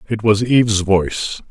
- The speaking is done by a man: Yes, male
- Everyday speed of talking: Yes, average, 160 wpm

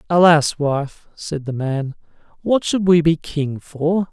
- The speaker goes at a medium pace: Yes, average, 160 wpm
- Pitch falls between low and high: Yes, medium, 155 Hz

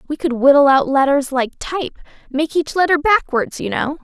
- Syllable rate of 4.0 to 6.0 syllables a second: Yes, 5.1 syllables/s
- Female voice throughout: Yes, female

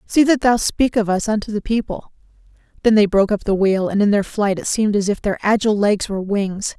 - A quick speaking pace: Yes, fast, 245 wpm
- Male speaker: No, female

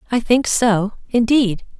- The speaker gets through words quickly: No, slow, 135 wpm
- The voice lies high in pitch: Yes, high, 225 Hz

